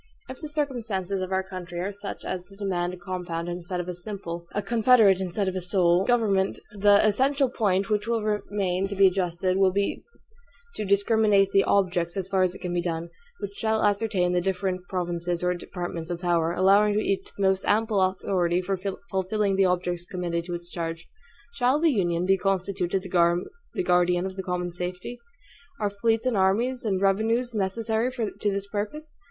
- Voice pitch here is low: No, high, 190 Hz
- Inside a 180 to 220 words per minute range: Yes, average, 190 wpm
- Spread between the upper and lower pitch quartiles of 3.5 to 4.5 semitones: No, average, 2.8 semitones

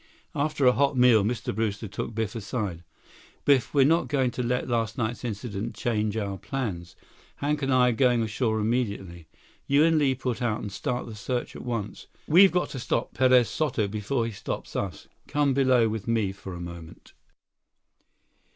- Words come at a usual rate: Yes, average, 180 wpm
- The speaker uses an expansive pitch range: No, average, 3.8 semitones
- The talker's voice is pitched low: Yes, low, 120 Hz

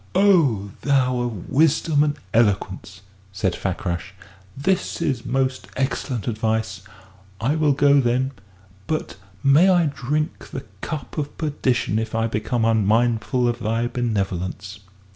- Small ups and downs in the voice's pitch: No, average, 4.6 semitones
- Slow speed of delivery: Yes, slow, 125 wpm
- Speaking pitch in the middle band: No, low, 120 Hz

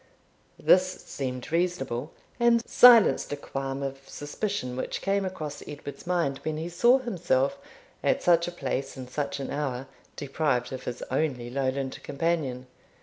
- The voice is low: No, medium, 145 Hz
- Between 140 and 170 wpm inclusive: Yes, average, 145 wpm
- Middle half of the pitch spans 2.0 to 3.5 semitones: No, average, 4.7 semitones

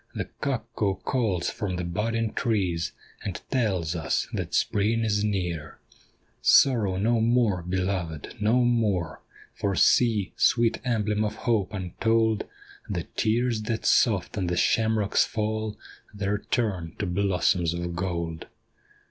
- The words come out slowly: Yes, slow, 130 wpm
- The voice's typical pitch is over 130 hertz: No, low, 105 Hz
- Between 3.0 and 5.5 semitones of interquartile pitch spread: Yes, average, 3.8 semitones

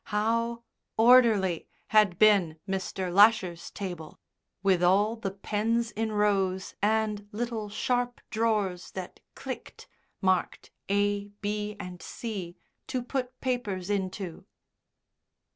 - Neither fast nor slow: No, slow, 110 wpm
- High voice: Yes, high, 205 Hz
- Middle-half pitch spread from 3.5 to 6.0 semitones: No, average, 3.0 semitones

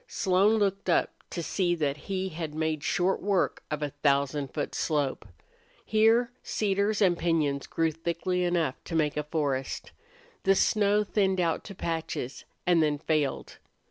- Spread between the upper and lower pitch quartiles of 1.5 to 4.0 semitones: No, average, 4.4 semitones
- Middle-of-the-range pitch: Yes, medium, 170 Hz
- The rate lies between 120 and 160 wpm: Yes, average, 155 wpm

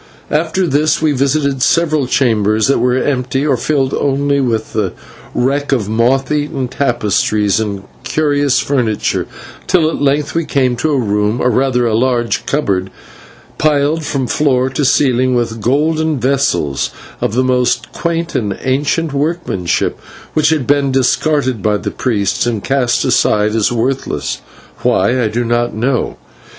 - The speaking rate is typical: Yes, average, 150 wpm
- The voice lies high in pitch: No, low, 130 Hz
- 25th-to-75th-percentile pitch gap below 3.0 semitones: No, average, 3.6 semitones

